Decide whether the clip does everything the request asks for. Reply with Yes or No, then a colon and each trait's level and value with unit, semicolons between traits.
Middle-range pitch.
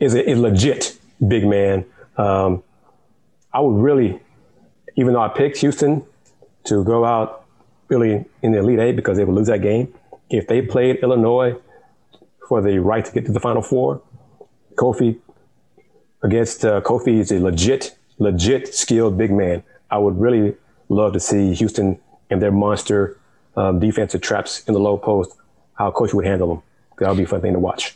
No: low, 110 Hz